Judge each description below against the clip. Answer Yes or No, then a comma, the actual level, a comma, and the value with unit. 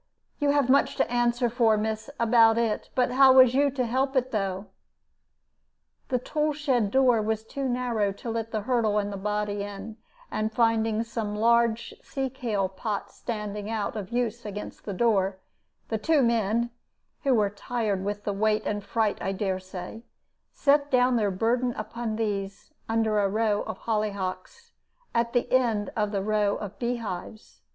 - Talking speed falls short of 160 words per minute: No, average, 175 wpm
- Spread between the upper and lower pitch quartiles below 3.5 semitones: Yes, average, 2.8 semitones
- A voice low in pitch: No, high, 225 Hz